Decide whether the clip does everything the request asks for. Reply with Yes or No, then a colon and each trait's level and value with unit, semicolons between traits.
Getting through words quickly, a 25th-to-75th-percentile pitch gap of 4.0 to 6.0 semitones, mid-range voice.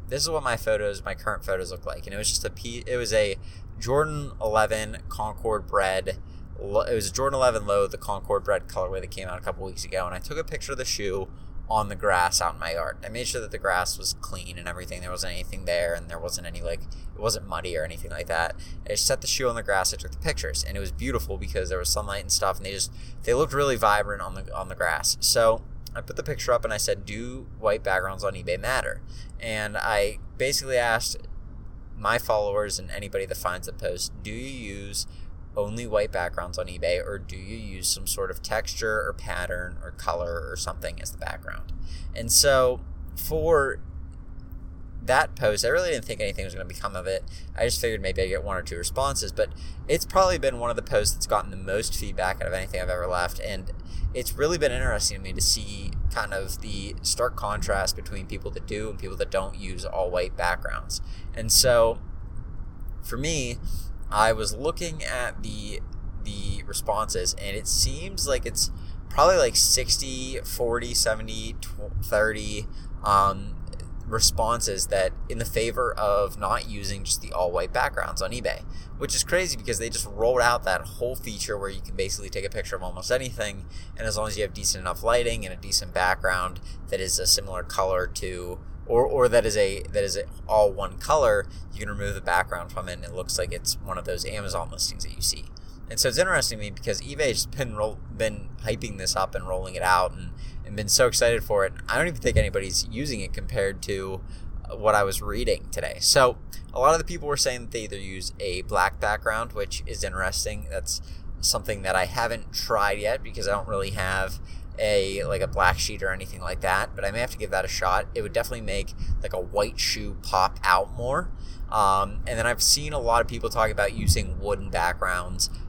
No: fast, 220 wpm; average, 4.4 semitones; low, 100 Hz